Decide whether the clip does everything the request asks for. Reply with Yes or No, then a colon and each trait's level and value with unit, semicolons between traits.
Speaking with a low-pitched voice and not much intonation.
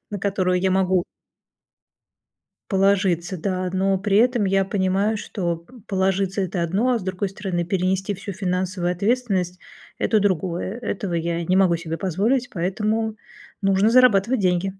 No: high, 190 Hz; narrow, 2.0 semitones